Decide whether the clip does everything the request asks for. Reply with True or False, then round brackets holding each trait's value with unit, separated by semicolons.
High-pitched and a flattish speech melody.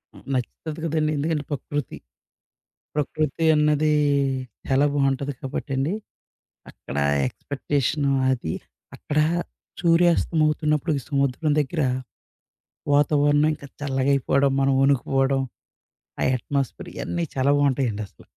False (145 Hz; 2.0 semitones)